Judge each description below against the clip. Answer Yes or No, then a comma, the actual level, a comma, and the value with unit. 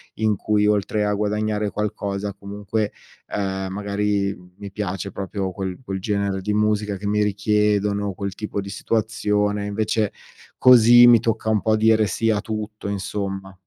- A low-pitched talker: Yes, low, 105 Hz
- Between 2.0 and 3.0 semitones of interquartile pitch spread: No, narrow, 1.3 semitones